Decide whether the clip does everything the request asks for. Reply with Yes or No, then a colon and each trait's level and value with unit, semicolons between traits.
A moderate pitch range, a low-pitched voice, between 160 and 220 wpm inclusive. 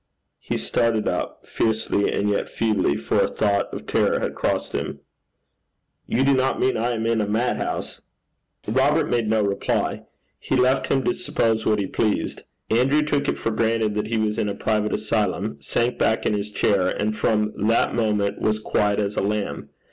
No: narrow, 2.1 semitones; low, 110 Hz; average, 185 wpm